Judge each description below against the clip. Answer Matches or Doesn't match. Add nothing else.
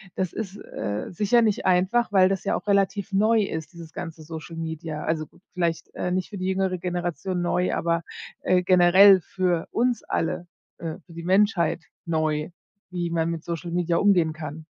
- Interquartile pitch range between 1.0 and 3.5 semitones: Matches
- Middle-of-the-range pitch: Matches